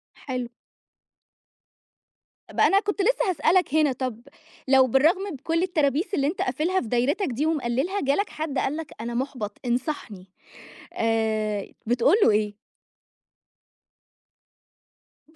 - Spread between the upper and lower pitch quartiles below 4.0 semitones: No, wide, 5.4 semitones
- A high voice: Yes, very high, 275 Hz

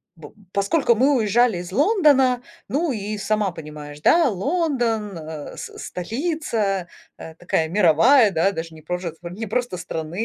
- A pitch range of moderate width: No, wide, 6.7 semitones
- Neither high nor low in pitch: No, high, 205 Hz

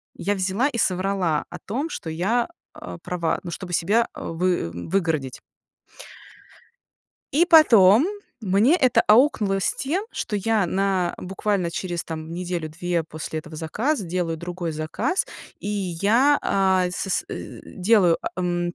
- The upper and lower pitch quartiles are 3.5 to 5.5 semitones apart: Yes, average, 4.0 semitones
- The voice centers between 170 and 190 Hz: Yes, medium, 185 Hz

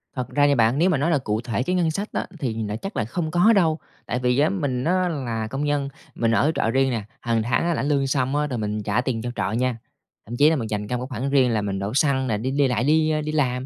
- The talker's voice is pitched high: No, low, 130 Hz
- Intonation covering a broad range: No, average, 4.5 semitones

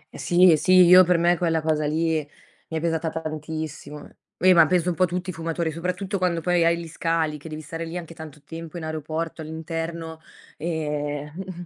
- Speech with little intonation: Yes, narrow, 1.7 semitones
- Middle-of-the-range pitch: Yes, medium, 165 Hz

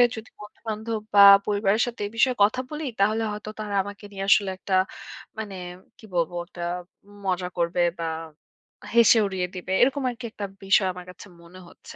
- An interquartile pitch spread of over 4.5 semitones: No, average, 3.0 semitones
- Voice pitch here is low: No, high, 205 Hz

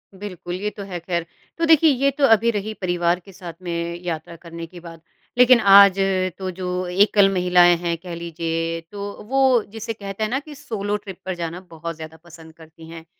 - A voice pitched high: No, medium, 180 Hz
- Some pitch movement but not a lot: Yes, average, 3.6 semitones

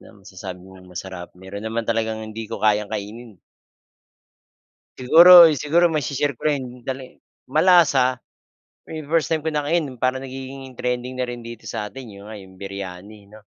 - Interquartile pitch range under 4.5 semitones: No, average, 5.0 semitones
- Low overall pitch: Yes, low, 120 Hz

